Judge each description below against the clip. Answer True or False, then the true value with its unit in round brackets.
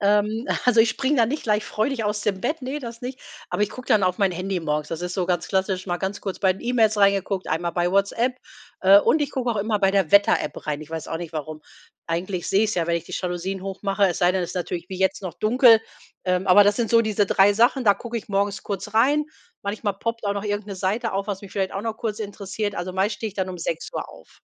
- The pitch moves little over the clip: False (3.0 semitones)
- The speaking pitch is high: True (200 Hz)